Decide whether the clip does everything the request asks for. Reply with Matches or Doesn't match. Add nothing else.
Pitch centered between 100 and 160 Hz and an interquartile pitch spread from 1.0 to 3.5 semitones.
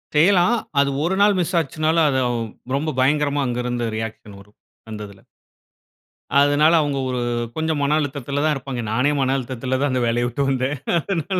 Doesn't match